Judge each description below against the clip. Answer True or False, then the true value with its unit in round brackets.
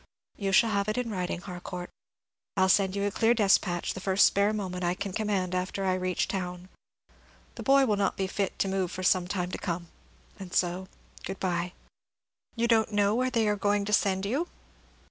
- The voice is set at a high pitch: True (195 Hz)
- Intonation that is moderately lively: False (2.2 semitones)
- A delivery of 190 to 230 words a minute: True (205 wpm)